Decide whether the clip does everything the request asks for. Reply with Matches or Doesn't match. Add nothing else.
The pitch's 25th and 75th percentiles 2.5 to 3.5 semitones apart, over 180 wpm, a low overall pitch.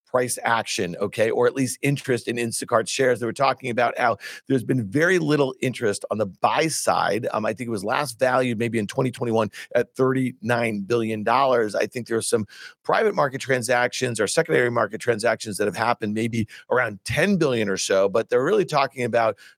Matches